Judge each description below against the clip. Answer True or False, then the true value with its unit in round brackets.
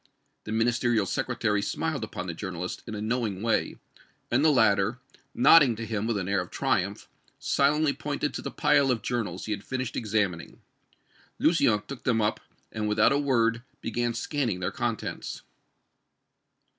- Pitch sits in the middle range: False (115 Hz)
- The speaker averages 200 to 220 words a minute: False (160 wpm)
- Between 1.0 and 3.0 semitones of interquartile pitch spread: False (3.9 semitones)